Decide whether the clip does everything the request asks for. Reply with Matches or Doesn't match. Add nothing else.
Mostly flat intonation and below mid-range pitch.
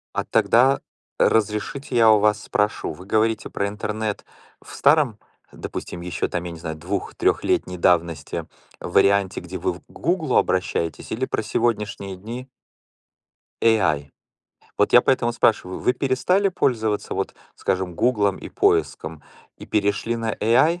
Doesn't match